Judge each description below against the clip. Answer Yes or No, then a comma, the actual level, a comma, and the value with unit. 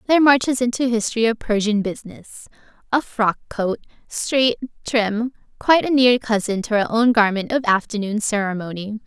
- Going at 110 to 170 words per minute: Yes, average, 145 wpm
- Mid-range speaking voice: No, high, 225 Hz